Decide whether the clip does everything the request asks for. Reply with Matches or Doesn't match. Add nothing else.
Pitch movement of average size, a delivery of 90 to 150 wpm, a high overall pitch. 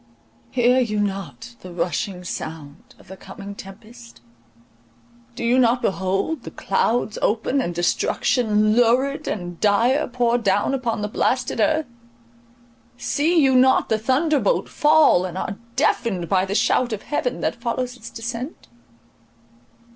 Matches